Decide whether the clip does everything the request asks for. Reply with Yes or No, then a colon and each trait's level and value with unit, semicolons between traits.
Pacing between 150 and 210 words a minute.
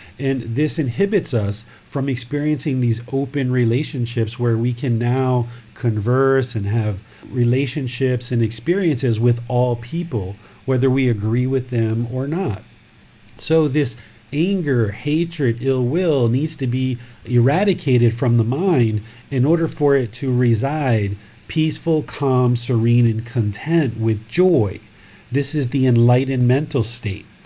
No: slow, 135 wpm